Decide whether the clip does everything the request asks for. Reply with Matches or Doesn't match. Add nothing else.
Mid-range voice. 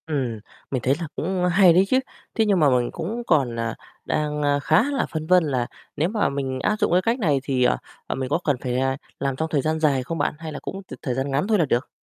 Matches